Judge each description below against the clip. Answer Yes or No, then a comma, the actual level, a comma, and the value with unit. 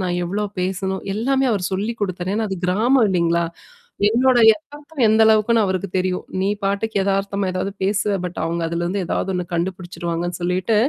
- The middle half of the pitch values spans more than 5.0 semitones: No, average, 3.2 semitones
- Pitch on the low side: No, high, 195 Hz